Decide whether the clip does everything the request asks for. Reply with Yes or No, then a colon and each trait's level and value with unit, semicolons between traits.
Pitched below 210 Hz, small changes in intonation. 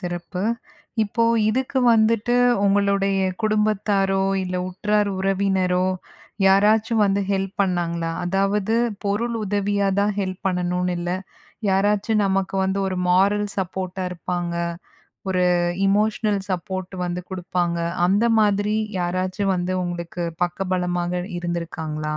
Yes: high, 190 Hz; narrow, 2.3 semitones